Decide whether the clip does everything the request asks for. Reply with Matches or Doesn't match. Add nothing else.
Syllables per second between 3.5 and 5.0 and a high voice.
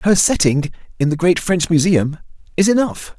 Doesn't match